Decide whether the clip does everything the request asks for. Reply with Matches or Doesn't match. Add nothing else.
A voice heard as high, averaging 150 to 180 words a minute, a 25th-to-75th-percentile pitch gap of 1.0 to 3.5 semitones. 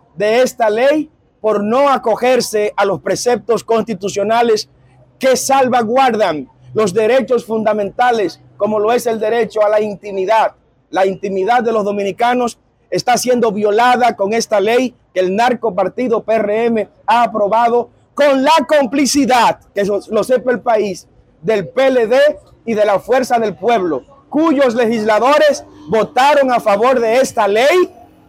Doesn't match